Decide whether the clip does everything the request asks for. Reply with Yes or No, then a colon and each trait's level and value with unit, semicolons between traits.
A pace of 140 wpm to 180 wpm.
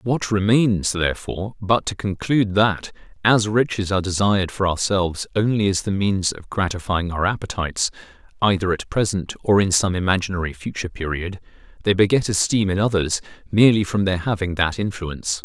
Yes: average, 160 wpm